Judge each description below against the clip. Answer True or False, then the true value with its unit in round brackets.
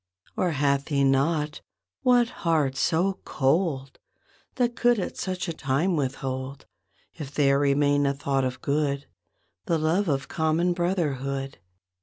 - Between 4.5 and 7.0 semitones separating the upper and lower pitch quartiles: False (3.9 semitones)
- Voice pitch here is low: False (145 Hz)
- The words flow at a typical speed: False (130 wpm)